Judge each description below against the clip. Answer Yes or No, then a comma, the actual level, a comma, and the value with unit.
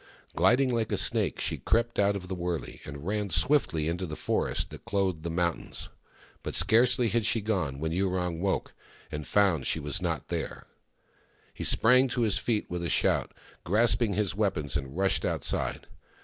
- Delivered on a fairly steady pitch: No, average, 4.9 semitones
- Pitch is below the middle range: Yes, very low, 95 Hz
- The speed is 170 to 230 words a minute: Yes, average, 175 wpm